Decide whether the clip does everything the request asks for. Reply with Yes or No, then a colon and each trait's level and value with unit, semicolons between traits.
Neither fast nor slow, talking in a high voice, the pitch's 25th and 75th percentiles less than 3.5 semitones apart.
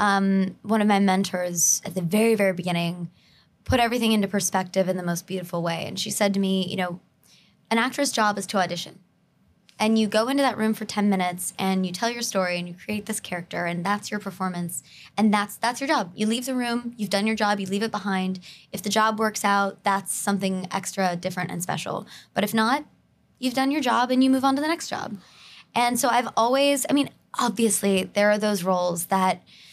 No: fast, 220 wpm; high, 200 Hz; average, 3.1 semitones